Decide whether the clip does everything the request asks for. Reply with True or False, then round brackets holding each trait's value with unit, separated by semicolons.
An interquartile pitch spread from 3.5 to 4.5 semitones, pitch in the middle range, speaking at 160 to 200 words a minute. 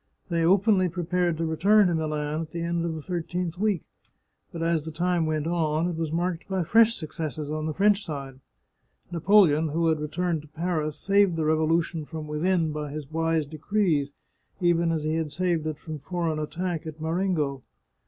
False (2.5 semitones; 165 Hz; 185 wpm)